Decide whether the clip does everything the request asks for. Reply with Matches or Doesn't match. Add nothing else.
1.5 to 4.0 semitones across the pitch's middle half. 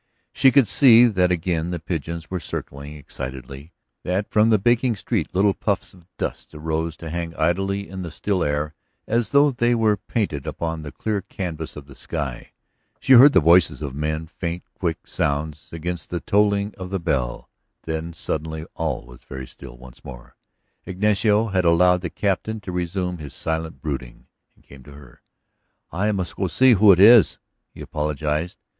Doesn't match